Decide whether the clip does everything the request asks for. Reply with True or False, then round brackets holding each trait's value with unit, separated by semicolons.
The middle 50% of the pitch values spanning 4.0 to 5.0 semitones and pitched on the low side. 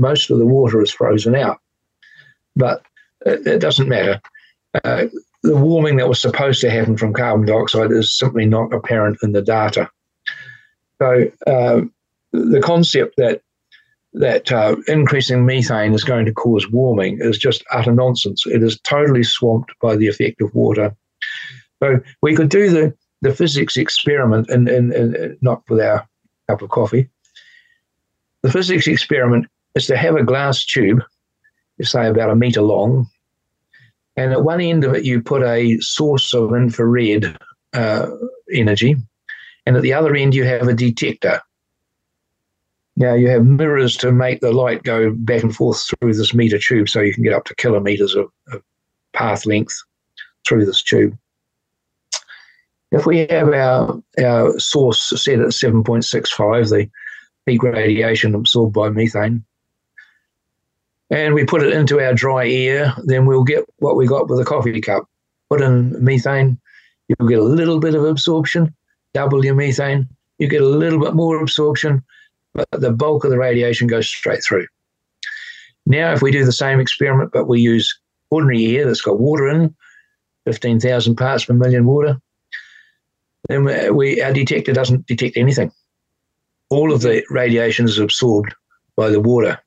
True (4.4 semitones; 125 Hz)